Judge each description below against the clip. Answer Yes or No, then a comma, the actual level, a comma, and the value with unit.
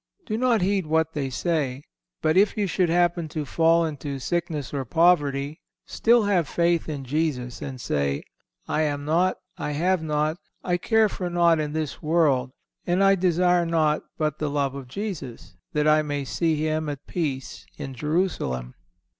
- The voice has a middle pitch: Yes, medium, 155 Hz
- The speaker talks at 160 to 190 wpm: Yes, average, 170 wpm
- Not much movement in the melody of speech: No, average, 3.4 semitones